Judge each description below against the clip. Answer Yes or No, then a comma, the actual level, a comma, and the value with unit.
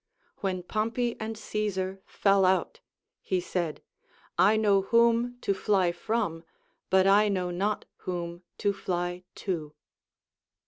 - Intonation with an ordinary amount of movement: Yes, average, 3.0 semitones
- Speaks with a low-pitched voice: No, high, 195 Hz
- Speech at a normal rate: No, slow, 125 wpm